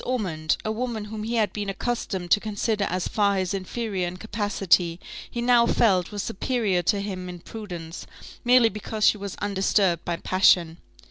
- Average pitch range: Yes, average, 3.2 semitones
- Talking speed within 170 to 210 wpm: Yes, average, 175 wpm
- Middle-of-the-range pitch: No, high, 200 Hz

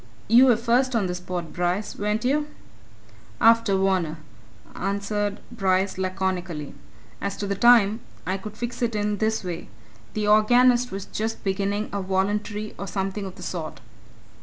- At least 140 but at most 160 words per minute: Yes, average, 155 wpm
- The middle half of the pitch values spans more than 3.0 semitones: No, average, 2.7 semitones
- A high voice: Yes, high, 205 Hz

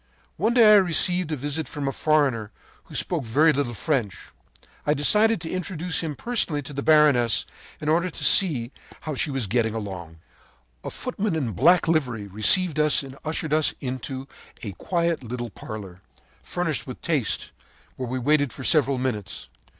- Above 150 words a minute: Yes, average, 170 wpm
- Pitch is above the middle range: No, medium, 145 Hz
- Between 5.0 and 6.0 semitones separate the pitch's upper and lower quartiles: Yes, average, 5.3 semitones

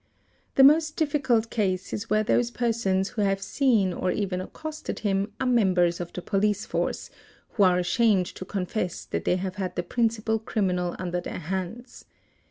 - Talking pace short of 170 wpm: No, average, 175 wpm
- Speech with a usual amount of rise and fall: Yes, average, 4.0 semitones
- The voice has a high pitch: Yes, high, 200 Hz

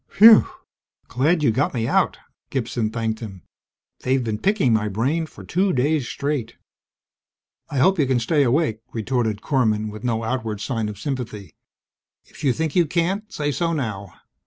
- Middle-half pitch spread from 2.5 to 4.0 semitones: No, wide, 5.5 semitones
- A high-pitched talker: No, low, 125 Hz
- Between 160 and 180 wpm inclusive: Yes, average, 165 wpm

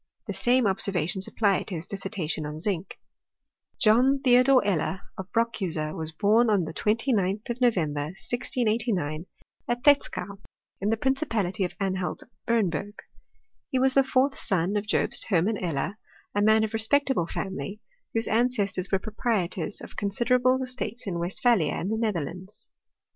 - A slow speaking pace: No, average, 155 wpm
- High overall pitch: Yes, high, 205 Hz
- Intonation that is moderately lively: Yes, average, 4.7 semitones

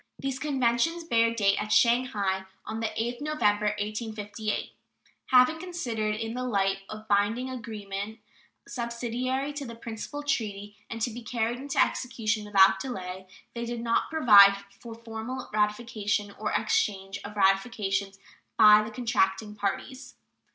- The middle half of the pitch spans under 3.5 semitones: Yes, average, 3.1 semitones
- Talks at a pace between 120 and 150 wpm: Yes, average, 145 wpm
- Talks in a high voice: Yes, high, 225 Hz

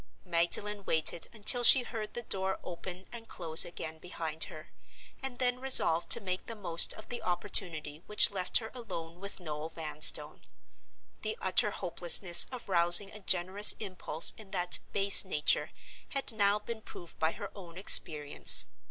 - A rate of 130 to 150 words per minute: No, average, 160 wpm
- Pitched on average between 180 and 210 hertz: Yes, medium, 185 Hz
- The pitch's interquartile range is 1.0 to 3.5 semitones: No, average, 4.0 semitones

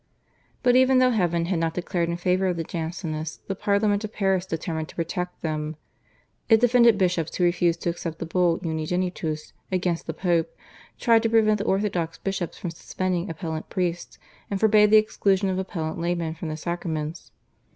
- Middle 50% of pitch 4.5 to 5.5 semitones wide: No, average, 3.2 semitones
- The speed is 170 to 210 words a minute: Yes, average, 180 wpm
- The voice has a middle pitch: Yes, medium, 180 Hz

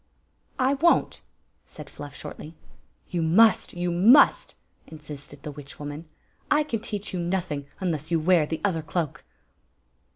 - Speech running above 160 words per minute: No, average, 155 wpm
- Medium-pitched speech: Yes, medium, 170 Hz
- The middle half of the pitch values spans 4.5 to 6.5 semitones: Yes, average, 5.1 semitones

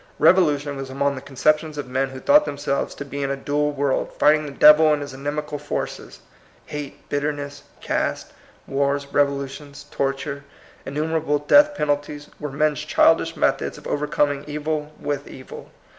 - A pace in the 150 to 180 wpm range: Yes, average, 165 wpm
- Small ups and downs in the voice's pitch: Yes, narrow, 1.2 semitones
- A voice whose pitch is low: No, medium, 145 Hz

